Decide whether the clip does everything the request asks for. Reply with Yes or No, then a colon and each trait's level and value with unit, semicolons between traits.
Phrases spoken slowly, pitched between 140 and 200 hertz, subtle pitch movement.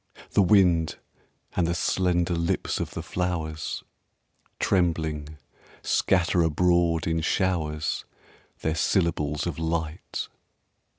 No: slow, 100 wpm; very low, 85 Hz; narrow, 2.1 semitones